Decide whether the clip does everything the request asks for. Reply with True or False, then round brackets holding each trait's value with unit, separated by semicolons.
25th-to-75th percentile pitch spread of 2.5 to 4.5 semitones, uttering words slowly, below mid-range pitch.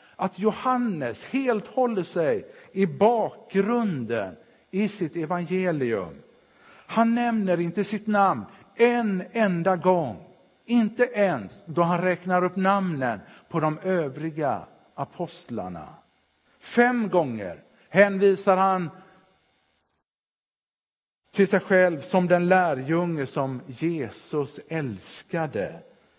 False (4.0 semitones; 95 wpm; 185 Hz)